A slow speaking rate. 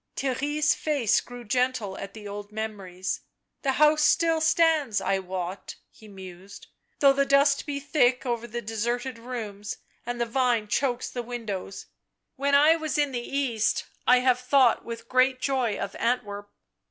No: average, 175 wpm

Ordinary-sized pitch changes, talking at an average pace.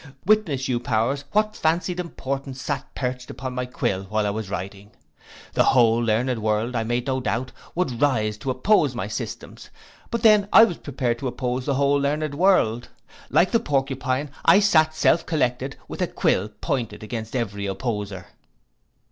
Yes: average, 4.6 semitones; average, 170 wpm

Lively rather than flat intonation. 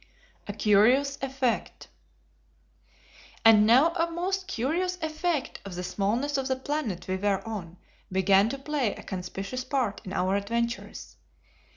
Yes: wide, 6.4 semitones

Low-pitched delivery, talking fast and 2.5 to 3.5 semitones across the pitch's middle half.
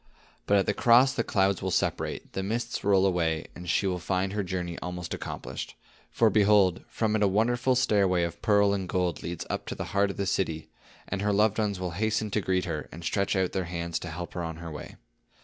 Yes: very low, 95 Hz; fast, 230 wpm; average, 2.9 semitones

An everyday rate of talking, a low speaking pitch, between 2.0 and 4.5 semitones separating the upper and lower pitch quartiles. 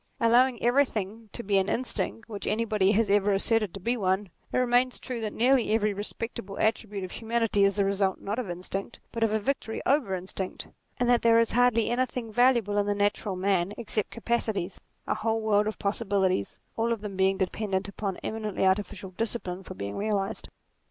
No: average, 185 wpm; high, 210 Hz; average, 2.8 semitones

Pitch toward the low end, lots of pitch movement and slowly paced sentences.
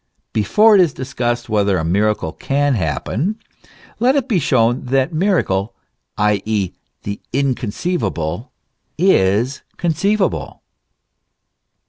Yes: low, 125 Hz; wide, 9.0 semitones; slow, 100 wpm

